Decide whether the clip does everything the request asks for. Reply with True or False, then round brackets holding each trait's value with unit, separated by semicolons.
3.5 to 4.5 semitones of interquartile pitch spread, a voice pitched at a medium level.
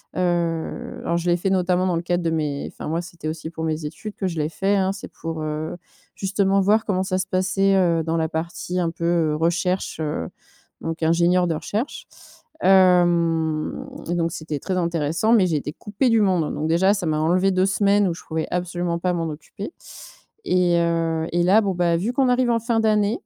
False (2.8 semitones; 175 Hz)